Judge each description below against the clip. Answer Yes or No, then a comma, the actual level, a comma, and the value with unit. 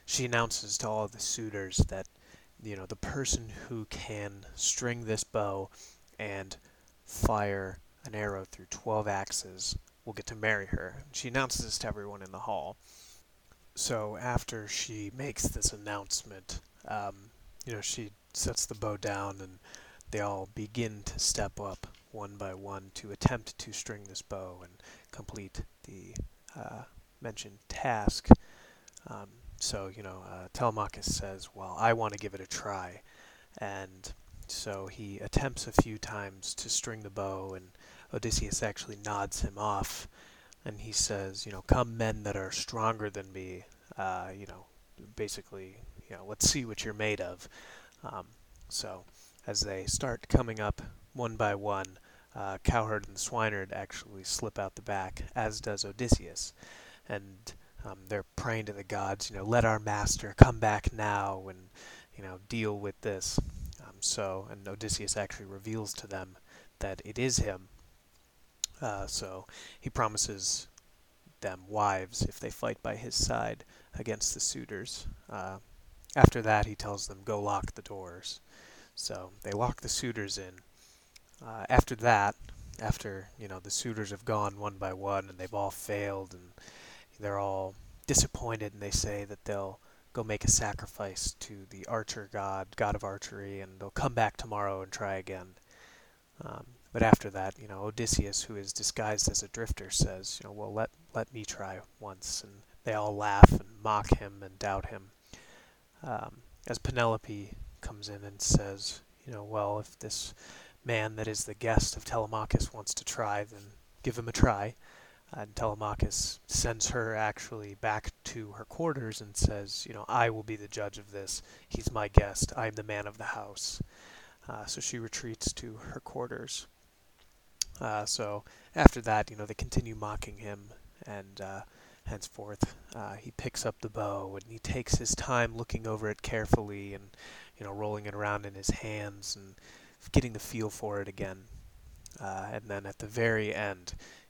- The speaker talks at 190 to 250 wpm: No, average, 170 wpm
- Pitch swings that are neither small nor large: No, narrow, 2.2 semitones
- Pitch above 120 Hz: No, low, 105 Hz